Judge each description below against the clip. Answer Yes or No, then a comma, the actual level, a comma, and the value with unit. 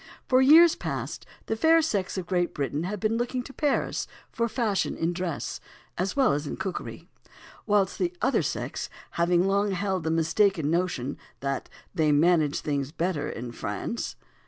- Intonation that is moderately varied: No, wide, 5.9 semitones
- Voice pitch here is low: No, medium, 180 Hz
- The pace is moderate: Yes, average, 165 wpm